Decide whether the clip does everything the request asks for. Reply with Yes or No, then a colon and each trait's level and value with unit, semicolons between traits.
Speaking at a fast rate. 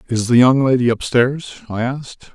No: average, 180 wpm